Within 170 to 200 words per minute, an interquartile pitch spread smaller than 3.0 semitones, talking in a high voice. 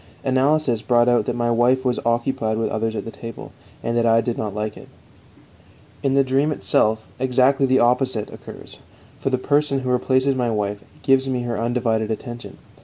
No: average, 180 wpm; narrow, 2.6 semitones; low, 120 Hz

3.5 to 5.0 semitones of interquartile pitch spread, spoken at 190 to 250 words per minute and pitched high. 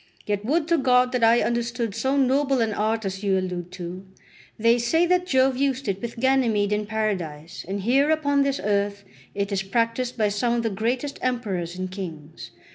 Yes: average, 4.7 semitones; average, 195 wpm; high, 225 Hz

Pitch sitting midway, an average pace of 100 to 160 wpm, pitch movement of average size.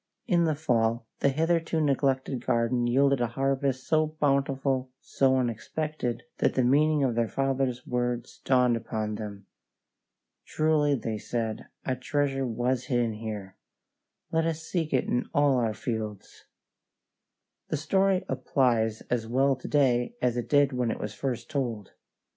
No: low, 130 Hz; average, 150 wpm; average, 3.2 semitones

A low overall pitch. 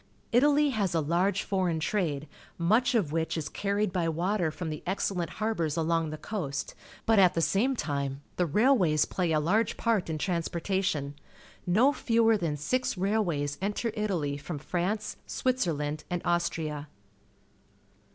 No: medium, 175 Hz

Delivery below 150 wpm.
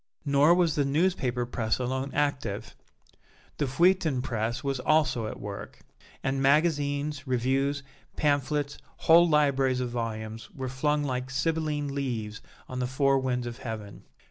Yes: average, 140 wpm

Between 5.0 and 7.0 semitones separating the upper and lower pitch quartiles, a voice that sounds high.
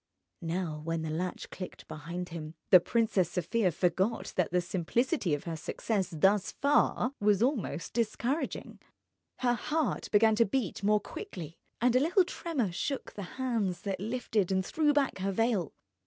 Yes: wide, 5.4 semitones; high, 200 Hz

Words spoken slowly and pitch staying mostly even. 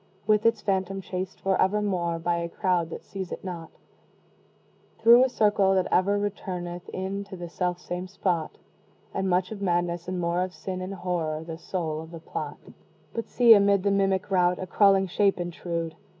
No: average, 185 wpm; narrow, 2.2 semitones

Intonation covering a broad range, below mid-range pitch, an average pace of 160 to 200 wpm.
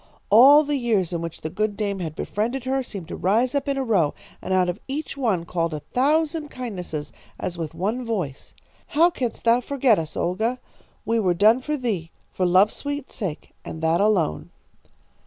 No: wide, 6.6 semitones; high, 215 Hz; average, 195 wpm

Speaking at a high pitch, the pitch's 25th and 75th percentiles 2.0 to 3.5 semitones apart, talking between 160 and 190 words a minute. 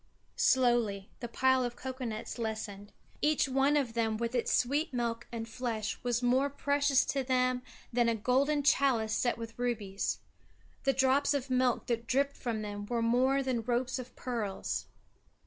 Yes: high, 245 Hz; narrow, 2.4 semitones; average, 165 wpm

